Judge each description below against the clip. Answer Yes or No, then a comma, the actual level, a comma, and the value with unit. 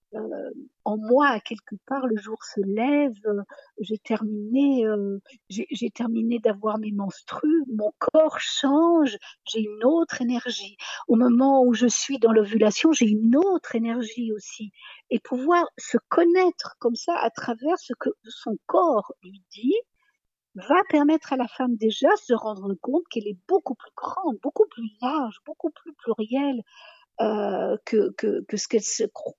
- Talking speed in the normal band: Yes, average, 165 wpm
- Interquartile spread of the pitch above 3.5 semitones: Yes, average, 5.2 semitones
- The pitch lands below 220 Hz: No, high, 240 Hz